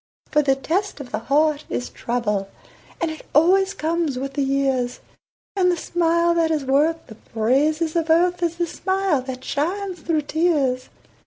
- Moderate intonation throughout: Yes, average, 4.1 semitones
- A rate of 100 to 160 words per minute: No, average, 170 wpm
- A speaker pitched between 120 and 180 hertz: No, very high, 310 Hz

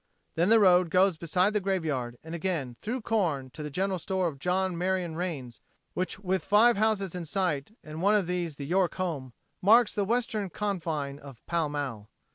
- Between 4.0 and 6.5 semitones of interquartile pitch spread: Yes, average, 4.3 semitones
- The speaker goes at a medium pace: Yes, average, 190 wpm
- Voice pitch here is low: No, medium, 180 Hz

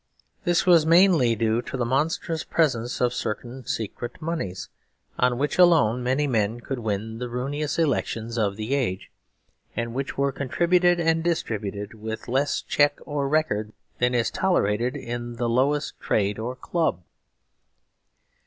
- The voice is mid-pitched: No, low, 125 Hz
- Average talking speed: Yes, average, 145 wpm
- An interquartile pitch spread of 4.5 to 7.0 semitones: Yes, average, 4.9 semitones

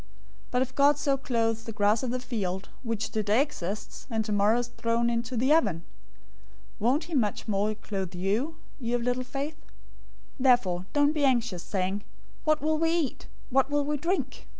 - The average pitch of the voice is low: No, high, 235 Hz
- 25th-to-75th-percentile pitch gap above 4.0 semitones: Yes, average, 4.9 semitones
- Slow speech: No, average, 185 wpm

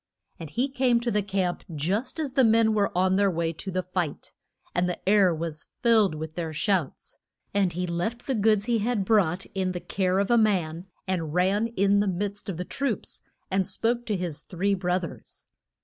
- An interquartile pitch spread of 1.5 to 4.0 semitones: Yes, average, 3.5 semitones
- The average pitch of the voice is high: Yes, high, 195 Hz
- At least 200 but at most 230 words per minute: Yes, fast, 205 wpm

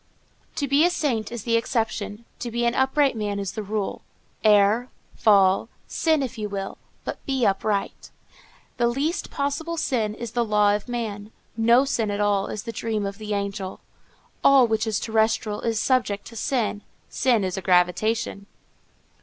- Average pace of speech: Yes, average, 170 wpm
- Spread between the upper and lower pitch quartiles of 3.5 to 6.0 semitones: No, average, 3.0 semitones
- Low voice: No, high, 220 Hz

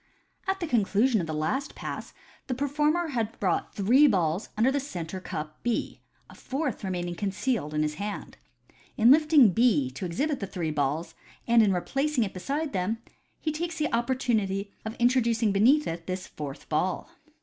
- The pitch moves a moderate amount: No, wide, 7.0 semitones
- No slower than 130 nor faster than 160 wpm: No, average, 180 wpm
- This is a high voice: Yes, high, 220 Hz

